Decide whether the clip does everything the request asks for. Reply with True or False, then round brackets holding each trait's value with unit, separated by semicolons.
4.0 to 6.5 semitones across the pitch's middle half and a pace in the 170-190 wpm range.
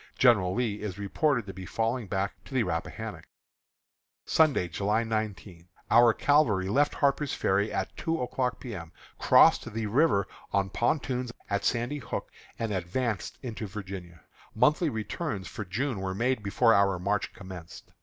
False (4.5 semitones; 155 wpm)